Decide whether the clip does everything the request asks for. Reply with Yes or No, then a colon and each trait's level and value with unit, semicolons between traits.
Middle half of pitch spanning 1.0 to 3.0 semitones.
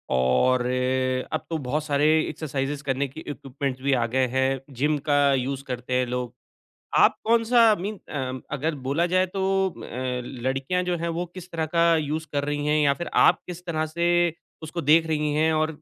No: average, 3.5 semitones